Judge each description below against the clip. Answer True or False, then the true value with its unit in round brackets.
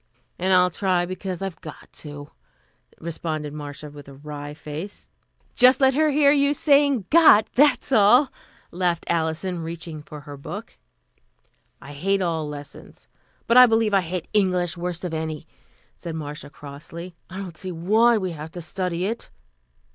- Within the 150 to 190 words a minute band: True (160 wpm)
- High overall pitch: False (175 Hz)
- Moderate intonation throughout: True (5.0 semitones)